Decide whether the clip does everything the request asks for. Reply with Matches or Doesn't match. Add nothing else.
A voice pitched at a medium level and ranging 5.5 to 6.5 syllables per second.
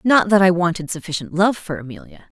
Matches